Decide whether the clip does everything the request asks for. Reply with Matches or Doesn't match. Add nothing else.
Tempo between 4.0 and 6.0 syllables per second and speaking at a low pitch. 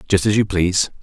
Doesn't match